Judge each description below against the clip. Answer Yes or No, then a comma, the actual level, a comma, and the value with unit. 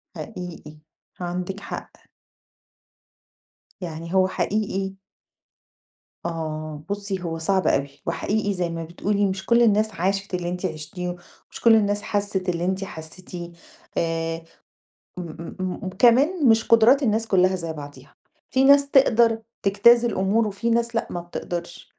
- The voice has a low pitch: No, high, 190 Hz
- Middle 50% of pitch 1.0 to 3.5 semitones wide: No, average, 4.1 semitones